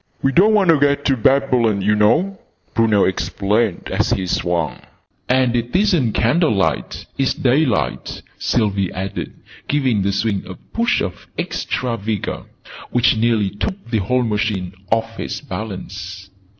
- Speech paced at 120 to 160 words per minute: Yes, average, 140 wpm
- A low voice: Yes, low, 115 Hz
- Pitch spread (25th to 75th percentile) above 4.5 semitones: Yes, average, 5.0 semitones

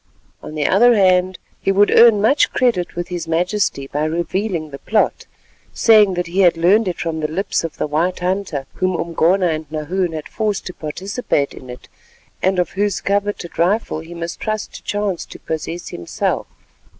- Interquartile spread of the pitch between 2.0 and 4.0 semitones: Yes, average, 3.7 semitones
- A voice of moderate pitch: Yes, medium, 180 Hz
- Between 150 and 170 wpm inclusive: No, average, 185 wpm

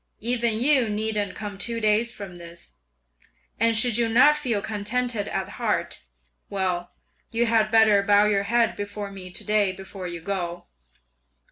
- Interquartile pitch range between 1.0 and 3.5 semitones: Yes, average, 2.8 semitones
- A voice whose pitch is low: No, high, 210 Hz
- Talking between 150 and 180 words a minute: Yes, average, 155 wpm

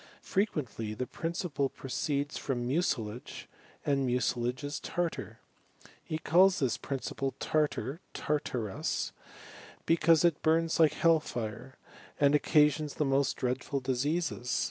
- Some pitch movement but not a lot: Yes, average, 4.0 semitones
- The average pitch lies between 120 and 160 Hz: Yes, medium, 140 Hz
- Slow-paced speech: Yes, slow, 110 wpm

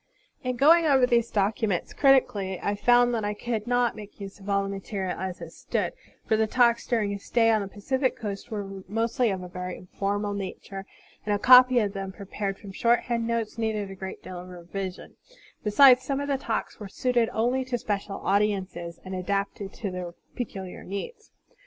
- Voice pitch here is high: Yes, high, 205 Hz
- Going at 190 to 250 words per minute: Yes, average, 195 wpm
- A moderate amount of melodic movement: Yes, average, 3.7 semitones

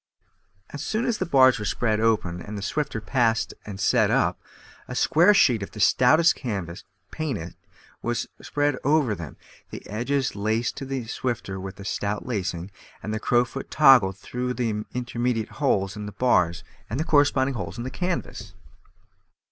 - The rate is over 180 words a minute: No, average, 165 wpm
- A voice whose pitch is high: No, low, 120 Hz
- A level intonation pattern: No, average, 4.8 semitones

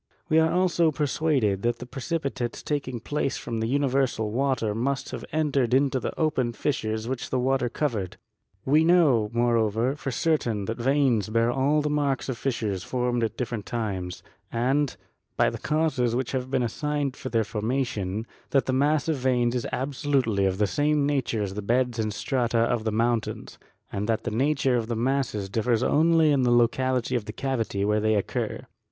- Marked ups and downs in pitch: No, average, 3.7 semitones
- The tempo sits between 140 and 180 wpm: No, average, 190 wpm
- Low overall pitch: Yes, low, 125 Hz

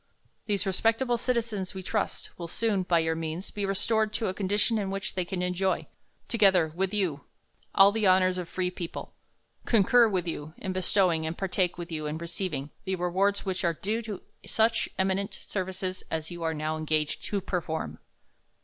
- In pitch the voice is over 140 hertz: Yes, medium, 185 Hz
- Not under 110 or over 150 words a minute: No, average, 185 wpm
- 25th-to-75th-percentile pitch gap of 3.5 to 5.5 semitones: No, average, 3.0 semitones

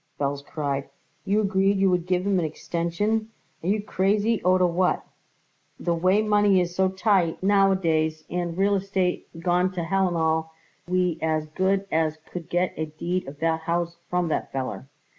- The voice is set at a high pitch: No, medium, 180 Hz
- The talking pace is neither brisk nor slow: Yes, average, 165 wpm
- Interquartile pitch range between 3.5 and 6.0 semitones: No, average, 3.0 semitones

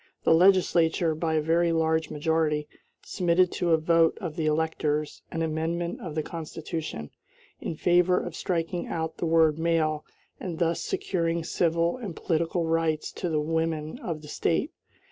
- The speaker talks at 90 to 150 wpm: No, average, 160 wpm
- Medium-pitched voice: Yes, medium, 165 Hz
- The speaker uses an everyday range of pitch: No, narrow, 1.4 semitones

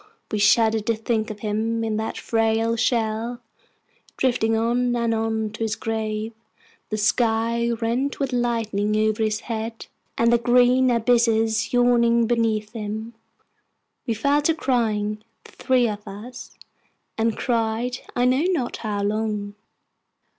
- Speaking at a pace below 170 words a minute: Yes, average, 140 wpm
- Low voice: No, high, 225 Hz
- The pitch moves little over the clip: Yes, narrow, 1.7 semitones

